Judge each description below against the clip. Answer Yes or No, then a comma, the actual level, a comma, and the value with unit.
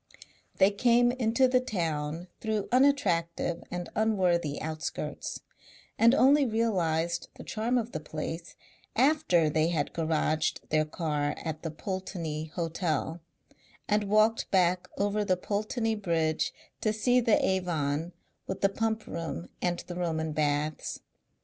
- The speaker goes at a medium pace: No, slow, 130 wpm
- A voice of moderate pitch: Yes, medium, 180 Hz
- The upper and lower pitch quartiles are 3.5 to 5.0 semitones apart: No, wide, 5.5 semitones